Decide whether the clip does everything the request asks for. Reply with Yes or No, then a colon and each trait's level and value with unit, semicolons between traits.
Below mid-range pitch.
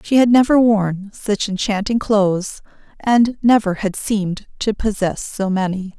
No: high, 205 Hz